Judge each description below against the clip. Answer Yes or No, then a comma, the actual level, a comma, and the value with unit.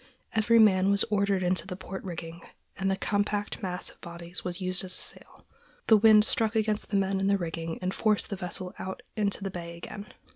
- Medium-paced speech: No, fast, 215 wpm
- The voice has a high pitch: Yes, high, 195 Hz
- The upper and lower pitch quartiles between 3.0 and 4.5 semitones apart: No, narrow, 2.4 semitones